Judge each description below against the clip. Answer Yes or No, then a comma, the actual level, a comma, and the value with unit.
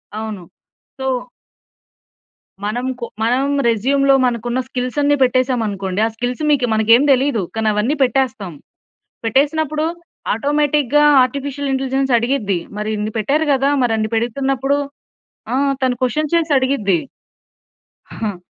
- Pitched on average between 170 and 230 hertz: No, very high, 255 Hz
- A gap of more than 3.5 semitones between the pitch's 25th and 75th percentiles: Yes, average, 3.9 semitones